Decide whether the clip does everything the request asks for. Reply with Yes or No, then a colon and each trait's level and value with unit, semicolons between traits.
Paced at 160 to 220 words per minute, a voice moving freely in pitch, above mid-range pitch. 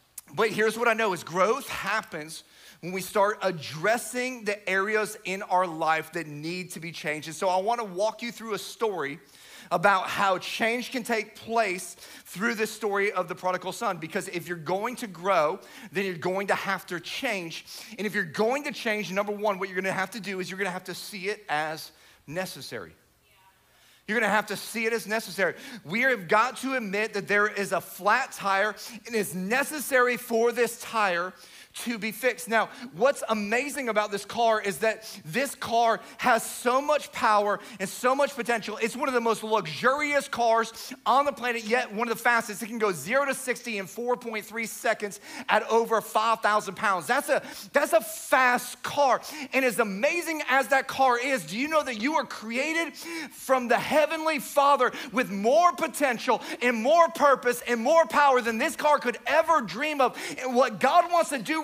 No: average, 200 wpm; average, 4.3 semitones; high, 225 Hz